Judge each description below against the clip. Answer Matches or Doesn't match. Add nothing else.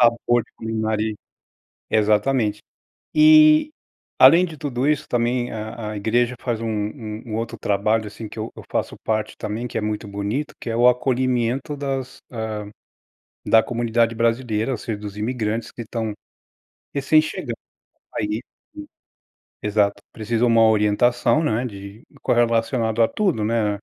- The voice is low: Matches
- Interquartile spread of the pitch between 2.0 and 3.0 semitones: Matches